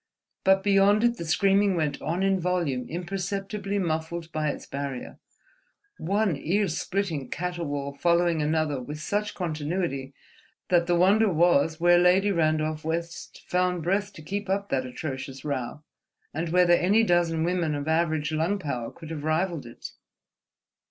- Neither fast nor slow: Yes, average, 150 wpm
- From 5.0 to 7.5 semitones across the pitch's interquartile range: No, average, 3.7 semitones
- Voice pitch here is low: No, medium, 170 Hz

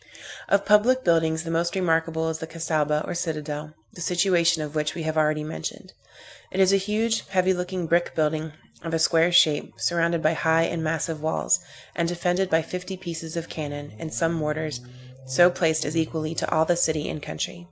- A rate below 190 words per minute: No, average, 195 wpm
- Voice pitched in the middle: Yes, medium, 165 Hz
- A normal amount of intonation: No, narrow, 2.0 semitones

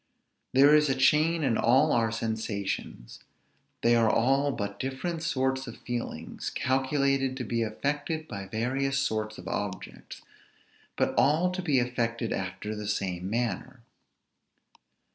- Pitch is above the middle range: No, low, 125 Hz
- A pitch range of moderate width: Yes, average, 4.1 semitones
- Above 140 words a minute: No, slow, 135 wpm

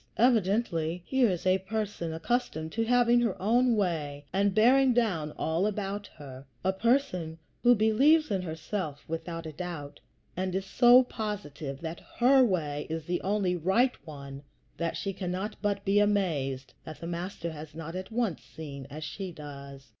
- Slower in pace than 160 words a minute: No, average, 165 wpm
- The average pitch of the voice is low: No, medium, 185 Hz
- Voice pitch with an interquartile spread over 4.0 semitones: Yes, wide, 5.4 semitones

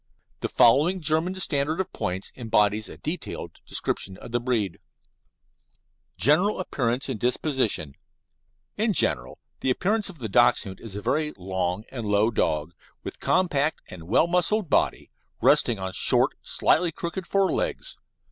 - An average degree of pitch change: No, wide, 8.8 semitones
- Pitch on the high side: No, low, 130 Hz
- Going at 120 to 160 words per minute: Yes, average, 140 wpm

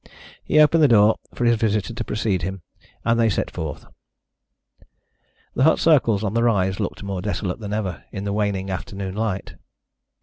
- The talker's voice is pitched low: Yes, low, 105 Hz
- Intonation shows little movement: No, average, 3.2 semitones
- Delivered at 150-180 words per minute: Yes, average, 175 wpm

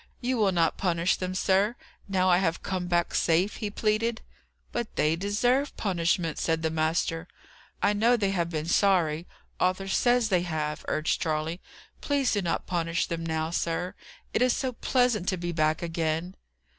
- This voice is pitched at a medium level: Yes, medium, 180 Hz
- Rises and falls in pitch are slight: No, average, 3.8 semitones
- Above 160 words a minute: Yes, average, 170 wpm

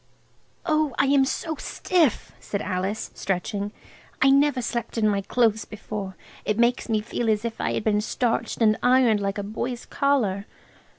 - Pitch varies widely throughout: No, average, 3.9 semitones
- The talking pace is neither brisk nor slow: Yes, average, 170 wpm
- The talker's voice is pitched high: Yes, high, 225 Hz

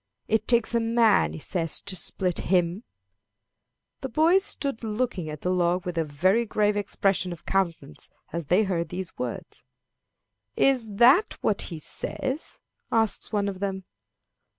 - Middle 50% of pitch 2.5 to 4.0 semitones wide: No, average, 4.5 semitones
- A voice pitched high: Yes, high, 195 Hz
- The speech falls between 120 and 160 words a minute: Yes, average, 150 wpm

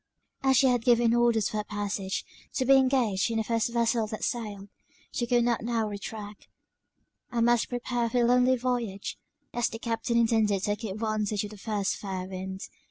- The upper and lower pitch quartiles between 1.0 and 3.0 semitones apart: Yes, narrow, 2.6 semitones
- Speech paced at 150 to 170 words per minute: No, average, 185 wpm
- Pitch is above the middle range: Yes, high, 225 Hz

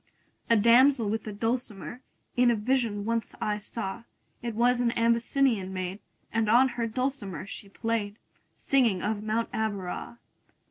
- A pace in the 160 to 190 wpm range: No, average, 150 wpm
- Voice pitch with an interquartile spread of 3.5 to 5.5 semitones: No, average, 2.8 semitones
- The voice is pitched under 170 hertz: No, high, 225 Hz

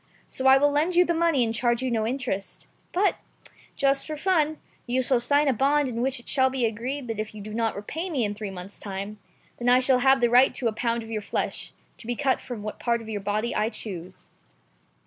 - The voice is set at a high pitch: Yes, high, 245 Hz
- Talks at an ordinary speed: No, fast, 245 wpm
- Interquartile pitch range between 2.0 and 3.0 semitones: No, average, 3.9 semitones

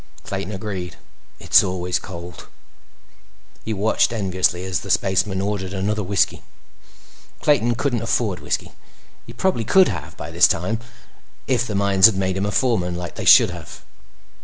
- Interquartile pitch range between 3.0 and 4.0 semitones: Yes, average, 3.5 semitones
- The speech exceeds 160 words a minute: No, average, 155 wpm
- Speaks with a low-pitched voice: Yes, very low, 95 Hz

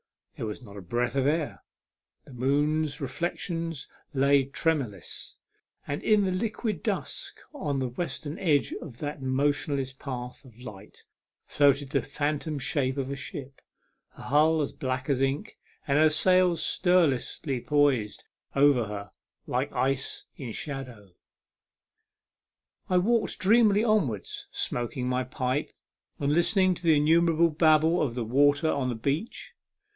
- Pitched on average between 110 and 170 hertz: Yes, medium, 140 Hz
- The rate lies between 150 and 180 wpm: No, average, 140 wpm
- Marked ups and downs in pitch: No, average, 3.9 semitones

